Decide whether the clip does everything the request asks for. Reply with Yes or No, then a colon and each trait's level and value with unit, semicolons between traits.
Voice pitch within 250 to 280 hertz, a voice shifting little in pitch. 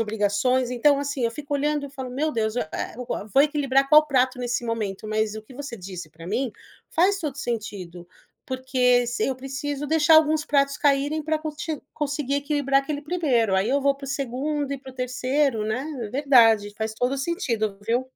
No: very high, 265 Hz; average, 3.9 semitones